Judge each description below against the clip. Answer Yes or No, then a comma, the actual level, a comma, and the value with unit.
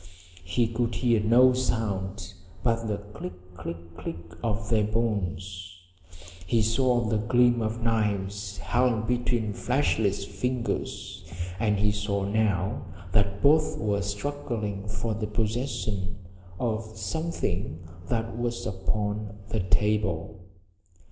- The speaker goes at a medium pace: No, slow, 115 wpm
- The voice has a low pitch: Yes, low, 105 Hz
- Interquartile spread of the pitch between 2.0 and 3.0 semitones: Yes, average, 2.7 semitones